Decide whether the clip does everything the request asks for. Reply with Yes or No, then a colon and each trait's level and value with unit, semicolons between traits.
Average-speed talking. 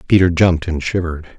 Yes: average, 175 wpm